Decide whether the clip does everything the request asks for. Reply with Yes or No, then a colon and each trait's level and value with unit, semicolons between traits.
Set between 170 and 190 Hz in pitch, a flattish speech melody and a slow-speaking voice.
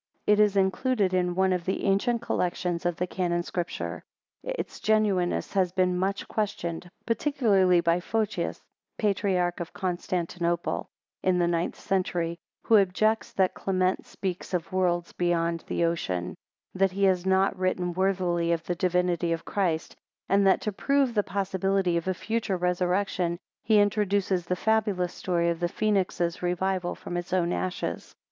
No: medium, 185 Hz; narrow, 2.1 semitones; average, 155 wpm